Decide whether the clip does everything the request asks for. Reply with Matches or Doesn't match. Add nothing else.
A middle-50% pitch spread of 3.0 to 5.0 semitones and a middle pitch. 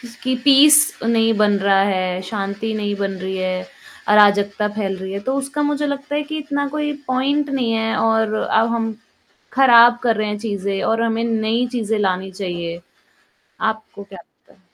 Doesn't match